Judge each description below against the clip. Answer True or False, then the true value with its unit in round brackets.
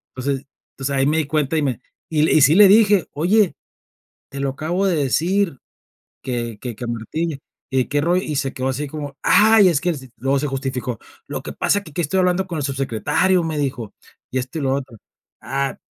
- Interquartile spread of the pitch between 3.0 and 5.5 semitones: True (4.4 semitones)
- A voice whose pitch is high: False (145 Hz)